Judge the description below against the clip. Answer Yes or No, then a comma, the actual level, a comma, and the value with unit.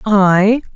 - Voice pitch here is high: Yes, high, 205 Hz